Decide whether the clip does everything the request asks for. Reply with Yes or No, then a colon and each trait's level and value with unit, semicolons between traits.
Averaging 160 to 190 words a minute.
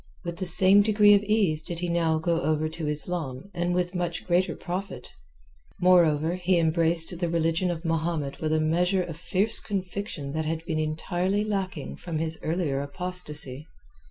Yes: average, 170 wpm